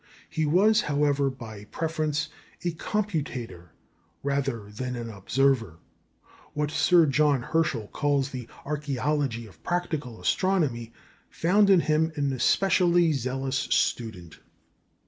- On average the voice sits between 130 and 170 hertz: Yes, medium, 140 Hz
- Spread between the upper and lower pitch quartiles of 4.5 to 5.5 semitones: Yes, average, 4.8 semitones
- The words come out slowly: Yes, slow, 110 wpm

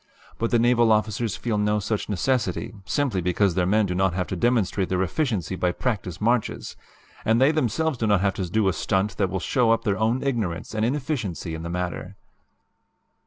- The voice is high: No, low, 105 Hz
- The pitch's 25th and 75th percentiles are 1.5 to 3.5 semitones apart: No, average, 4.3 semitones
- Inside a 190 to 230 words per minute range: Yes, average, 200 wpm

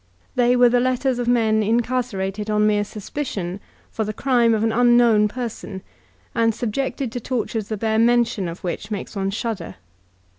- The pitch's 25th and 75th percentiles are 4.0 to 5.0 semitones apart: No, narrow, 2.5 semitones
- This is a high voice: Yes, high, 225 Hz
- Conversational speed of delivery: Yes, average, 170 wpm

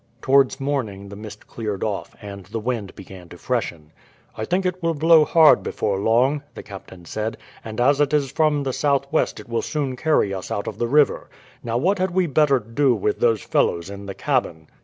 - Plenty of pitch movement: Yes, wide, 6.4 semitones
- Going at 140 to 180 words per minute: No, fast, 205 wpm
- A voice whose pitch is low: Yes, low, 120 Hz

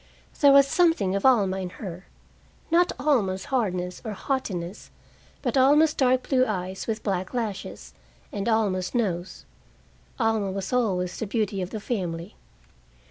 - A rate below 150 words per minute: Yes, average, 140 wpm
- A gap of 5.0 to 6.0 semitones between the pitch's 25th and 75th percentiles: Yes, average, 5.3 semitones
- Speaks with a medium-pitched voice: No, high, 210 Hz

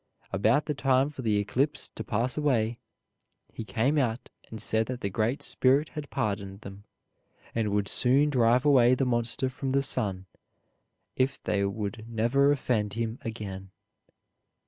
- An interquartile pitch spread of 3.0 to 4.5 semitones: Yes, average, 4.0 semitones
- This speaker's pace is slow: No, average, 155 wpm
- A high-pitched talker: No, low, 115 Hz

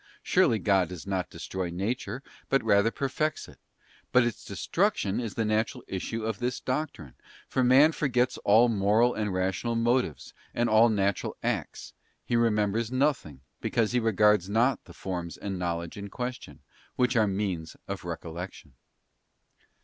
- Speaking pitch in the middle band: No, low, 110 Hz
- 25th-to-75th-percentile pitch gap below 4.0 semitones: No, average, 4.3 semitones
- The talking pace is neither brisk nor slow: Yes, average, 150 wpm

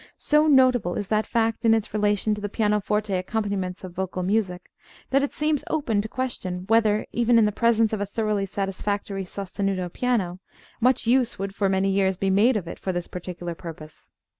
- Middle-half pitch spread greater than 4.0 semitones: No, average, 3.1 semitones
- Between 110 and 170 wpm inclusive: No, average, 190 wpm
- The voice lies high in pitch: Yes, high, 205 Hz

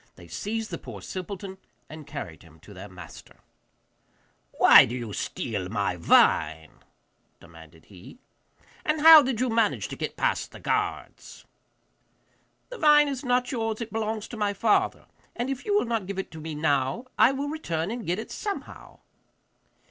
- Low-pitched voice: No, high, 210 Hz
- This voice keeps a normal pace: Yes, average, 175 wpm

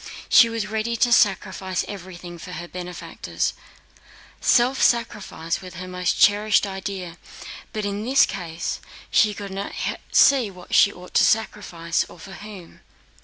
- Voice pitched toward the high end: Yes, high, 195 Hz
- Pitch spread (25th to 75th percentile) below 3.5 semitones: Yes, average, 2.9 semitones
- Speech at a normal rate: Yes, average, 145 wpm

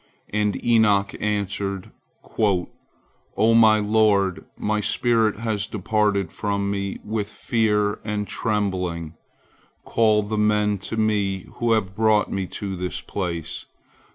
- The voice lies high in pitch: No, low, 105 Hz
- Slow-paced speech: Yes, slow, 120 wpm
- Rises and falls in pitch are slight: Yes, narrow, 1.6 semitones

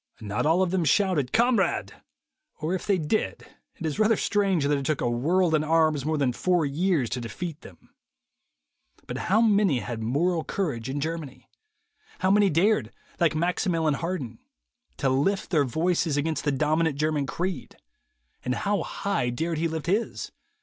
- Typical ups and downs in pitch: Yes, average, 4.6 semitones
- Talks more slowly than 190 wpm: Yes, average, 170 wpm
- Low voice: No, medium, 160 Hz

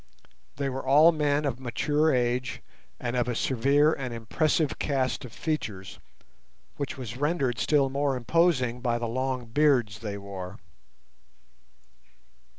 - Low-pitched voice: Yes, low, 130 Hz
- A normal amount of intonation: Yes, average, 3.5 semitones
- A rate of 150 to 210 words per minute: No, slow, 135 wpm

